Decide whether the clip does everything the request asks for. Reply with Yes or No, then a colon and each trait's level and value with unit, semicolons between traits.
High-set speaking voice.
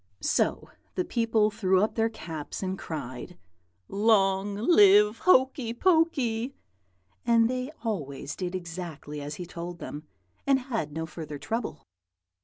Yes: high, 200 Hz